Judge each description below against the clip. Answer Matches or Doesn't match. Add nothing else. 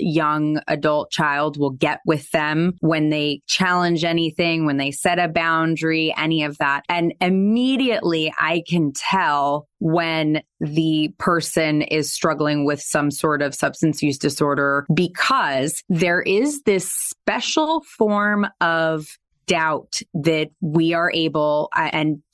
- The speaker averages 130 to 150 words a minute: Matches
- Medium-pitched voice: Matches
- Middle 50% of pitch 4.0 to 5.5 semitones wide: Doesn't match